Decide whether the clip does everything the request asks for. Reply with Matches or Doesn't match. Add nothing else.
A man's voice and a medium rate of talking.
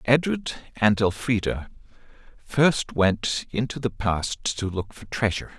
Doesn't match